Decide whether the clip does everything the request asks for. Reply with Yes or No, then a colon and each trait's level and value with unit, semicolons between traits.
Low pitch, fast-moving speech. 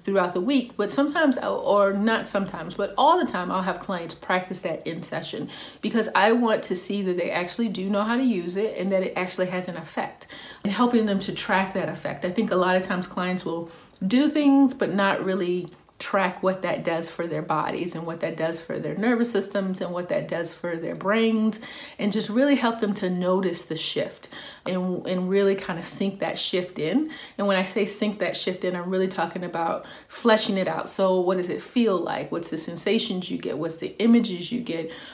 No: high, 190 Hz; fast, 225 wpm